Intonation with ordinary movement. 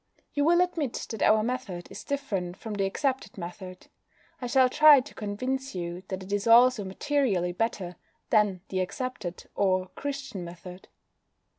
No: wide, 5.9 semitones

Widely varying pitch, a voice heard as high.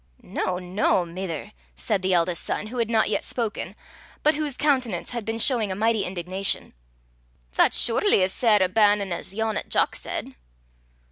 No: average, 3.8 semitones; high, 205 Hz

